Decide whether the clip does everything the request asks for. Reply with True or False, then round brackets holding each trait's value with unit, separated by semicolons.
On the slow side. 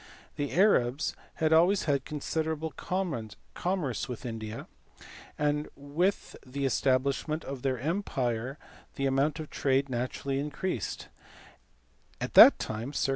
True (120 wpm)